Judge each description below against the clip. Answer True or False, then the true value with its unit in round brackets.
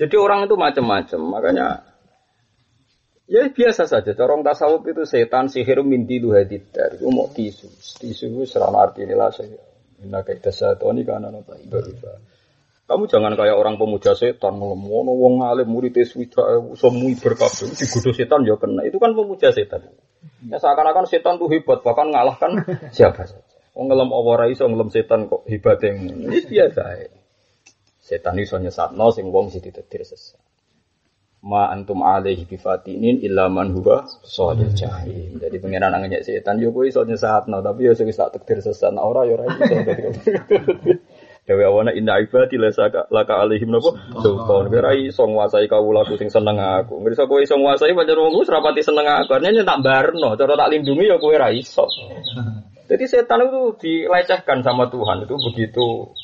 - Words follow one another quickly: True (170 wpm)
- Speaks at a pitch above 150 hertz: True (185 Hz)